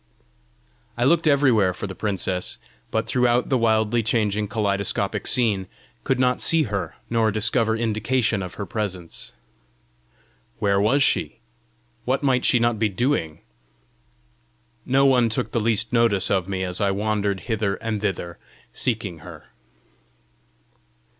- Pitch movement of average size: Yes, average, 3.3 semitones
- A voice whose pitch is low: Yes, low, 110 Hz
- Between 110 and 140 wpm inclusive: Yes, slow, 135 wpm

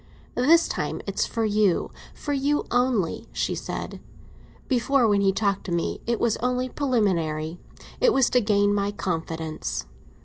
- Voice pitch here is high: Yes, high, 215 Hz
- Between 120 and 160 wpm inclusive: Yes, average, 140 wpm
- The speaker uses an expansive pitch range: No, average, 4.9 semitones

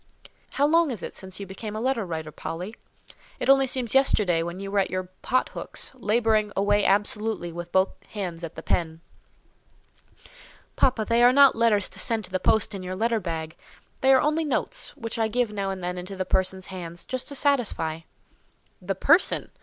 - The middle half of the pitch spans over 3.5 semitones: Yes, average, 4.8 semitones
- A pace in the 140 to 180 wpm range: No, average, 195 wpm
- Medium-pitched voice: No, high, 205 Hz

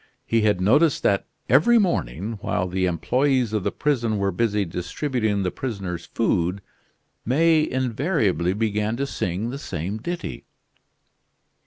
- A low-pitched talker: Yes, low, 110 Hz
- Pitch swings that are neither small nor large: No, wide, 5.9 semitones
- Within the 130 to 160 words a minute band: Yes, slow, 135 wpm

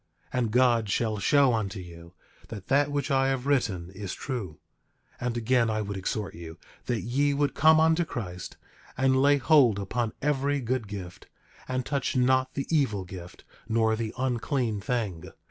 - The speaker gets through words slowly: No, average, 175 wpm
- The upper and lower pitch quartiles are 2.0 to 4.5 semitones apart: No, average, 5.0 semitones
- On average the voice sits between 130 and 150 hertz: No, low, 120 Hz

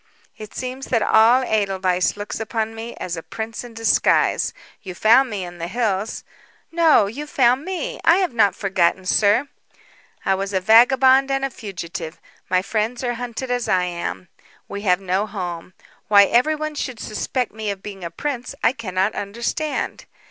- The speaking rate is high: No, average, 175 wpm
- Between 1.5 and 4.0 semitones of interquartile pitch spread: No, average, 4.6 semitones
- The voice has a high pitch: Yes, high, 220 Hz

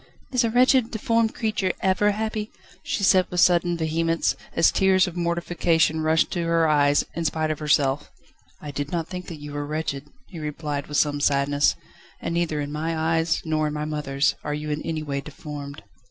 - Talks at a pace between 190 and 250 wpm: Yes, average, 195 wpm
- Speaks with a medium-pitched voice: Yes, medium, 160 Hz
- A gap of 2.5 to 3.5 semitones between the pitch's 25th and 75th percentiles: Yes, average, 3.0 semitones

